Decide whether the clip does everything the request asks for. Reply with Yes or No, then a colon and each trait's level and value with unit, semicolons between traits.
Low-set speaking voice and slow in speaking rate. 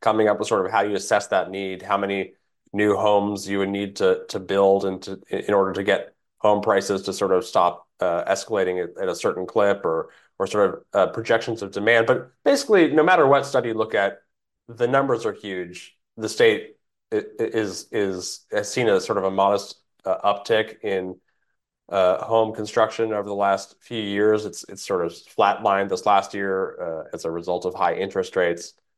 No: low, 105 Hz; fast, 205 wpm